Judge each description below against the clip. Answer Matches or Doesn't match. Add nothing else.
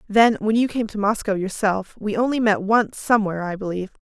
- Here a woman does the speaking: Matches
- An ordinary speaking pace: Doesn't match